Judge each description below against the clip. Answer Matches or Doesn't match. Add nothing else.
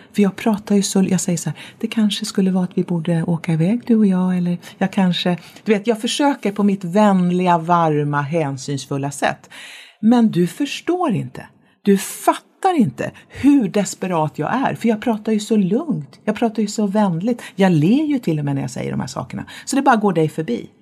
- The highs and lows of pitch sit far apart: Doesn't match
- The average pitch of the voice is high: Matches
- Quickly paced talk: Matches